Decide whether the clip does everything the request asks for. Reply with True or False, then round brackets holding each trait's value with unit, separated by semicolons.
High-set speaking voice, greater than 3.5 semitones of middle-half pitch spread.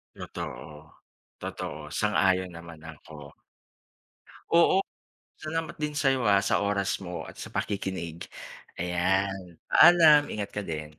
False (95 Hz; 4.3 semitones)